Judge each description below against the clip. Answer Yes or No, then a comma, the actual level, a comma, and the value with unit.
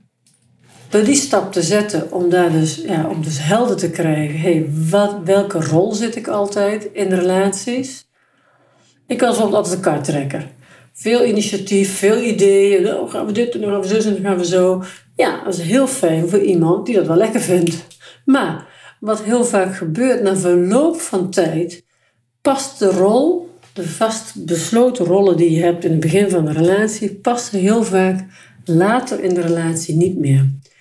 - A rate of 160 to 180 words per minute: Yes, average, 175 wpm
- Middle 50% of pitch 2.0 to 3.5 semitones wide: No, average, 3.9 semitones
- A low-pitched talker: No, high, 190 Hz